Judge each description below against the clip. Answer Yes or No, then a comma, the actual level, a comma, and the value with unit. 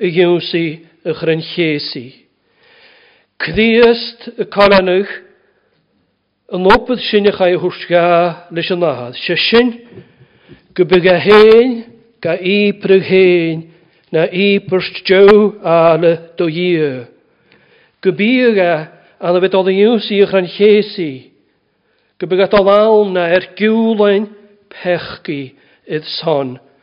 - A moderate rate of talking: No, slow, 110 wpm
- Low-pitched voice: No, medium, 185 Hz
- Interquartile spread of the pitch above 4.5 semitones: No, average, 3.7 semitones